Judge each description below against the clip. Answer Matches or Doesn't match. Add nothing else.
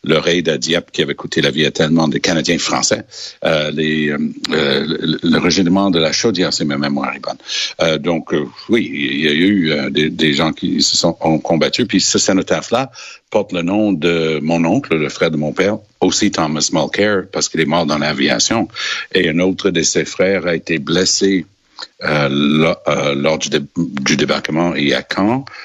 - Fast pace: Doesn't match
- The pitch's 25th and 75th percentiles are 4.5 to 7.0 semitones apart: Doesn't match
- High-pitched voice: Doesn't match